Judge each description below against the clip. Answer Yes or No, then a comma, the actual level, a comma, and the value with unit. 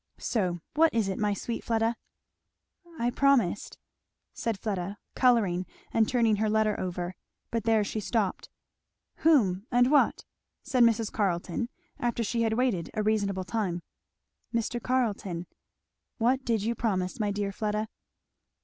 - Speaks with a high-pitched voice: Yes, high, 220 Hz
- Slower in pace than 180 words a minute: Yes, average, 140 wpm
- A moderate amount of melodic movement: Yes, average, 3.1 semitones